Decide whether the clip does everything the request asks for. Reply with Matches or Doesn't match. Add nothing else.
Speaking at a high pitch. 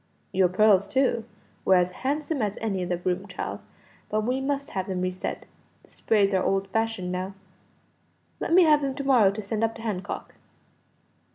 Matches